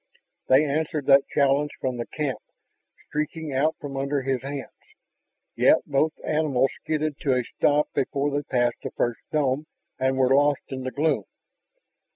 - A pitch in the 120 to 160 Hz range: Yes, medium, 140 Hz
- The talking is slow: No, average, 160 wpm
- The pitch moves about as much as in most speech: No, narrow, 2.1 semitones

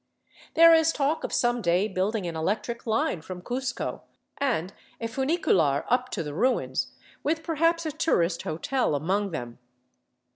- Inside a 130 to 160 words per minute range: Yes, average, 150 wpm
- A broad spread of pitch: Yes, wide, 8.5 semitones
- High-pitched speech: Yes, high, 225 Hz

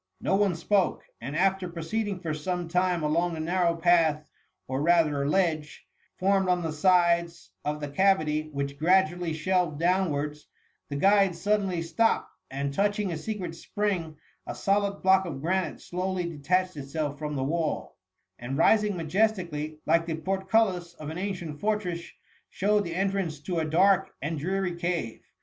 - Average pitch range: Yes, average, 3.6 semitones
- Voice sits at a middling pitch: Yes, medium, 175 Hz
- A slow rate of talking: No, average, 160 wpm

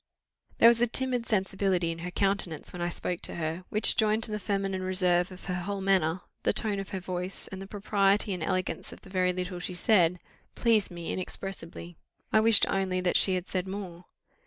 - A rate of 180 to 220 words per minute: Yes, fast, 205 wpm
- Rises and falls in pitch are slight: Yes, narrow, 2.1 semitones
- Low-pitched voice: No, high, 190 Hz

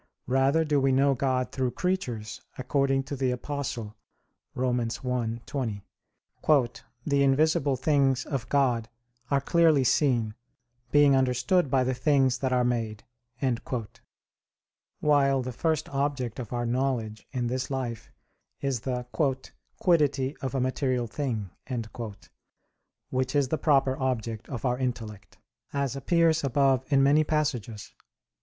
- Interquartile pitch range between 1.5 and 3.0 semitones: Yes, narrow, 2.4 semitones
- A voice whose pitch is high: No, low, 130 Hz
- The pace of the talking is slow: Yes, slow, 130 wpm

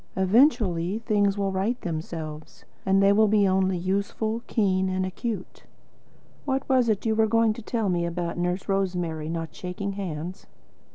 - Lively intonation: No, average, 3.5 semitones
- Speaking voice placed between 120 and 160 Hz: No, high, 190 Hz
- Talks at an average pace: Yes, average, 160 wpm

